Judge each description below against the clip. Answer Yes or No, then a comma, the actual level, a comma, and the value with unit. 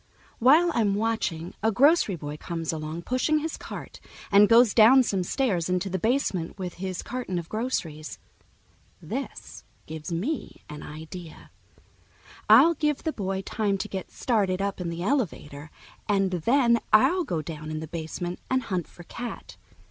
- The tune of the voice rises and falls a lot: Yes, wide, 6.3 semitones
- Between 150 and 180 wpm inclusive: Yes, average, 160 wpm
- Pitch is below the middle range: No, high, 195 Hz